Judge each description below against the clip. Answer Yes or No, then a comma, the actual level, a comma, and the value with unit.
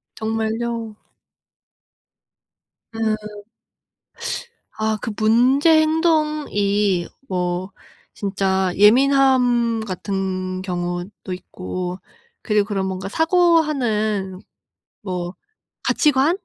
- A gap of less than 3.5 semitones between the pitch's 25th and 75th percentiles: No, wide, 5.5 semitones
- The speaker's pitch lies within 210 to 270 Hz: Yes, high, 215 Hz